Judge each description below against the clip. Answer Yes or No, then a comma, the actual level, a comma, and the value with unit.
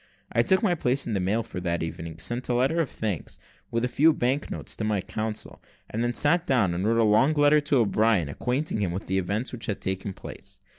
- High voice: No, low, 115 Hz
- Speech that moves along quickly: Yes, fast, 240 wpm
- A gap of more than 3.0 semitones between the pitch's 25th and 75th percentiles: Yes, wide, 5.5 semitones